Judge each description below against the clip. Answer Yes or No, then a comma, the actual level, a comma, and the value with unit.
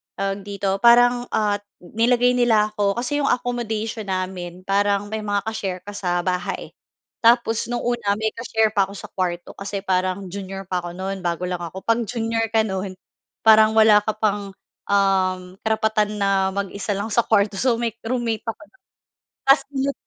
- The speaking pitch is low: No, high, 210 Hz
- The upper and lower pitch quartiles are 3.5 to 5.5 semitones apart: No, average, 2.8 semitones